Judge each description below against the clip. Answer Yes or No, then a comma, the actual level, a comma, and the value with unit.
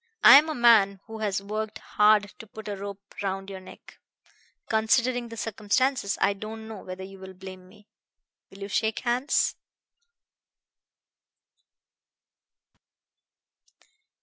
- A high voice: Yes, high, 210 Hz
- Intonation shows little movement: Yes, narrow, 2.2 semitones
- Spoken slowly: Yes, slow, 125 wpm